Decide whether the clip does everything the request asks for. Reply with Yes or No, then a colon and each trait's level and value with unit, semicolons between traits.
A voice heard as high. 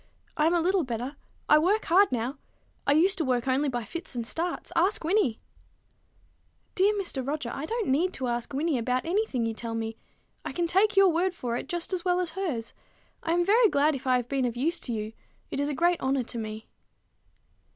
Yes: very high, 300 Hz